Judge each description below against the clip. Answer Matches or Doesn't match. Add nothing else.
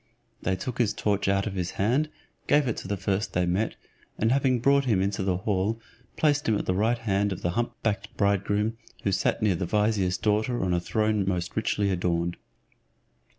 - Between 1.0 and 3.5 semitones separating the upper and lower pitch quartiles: Matches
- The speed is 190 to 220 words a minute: Matches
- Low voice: Matches